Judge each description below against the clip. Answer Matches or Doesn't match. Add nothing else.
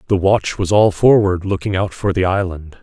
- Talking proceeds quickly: Matches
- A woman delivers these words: Doesn't match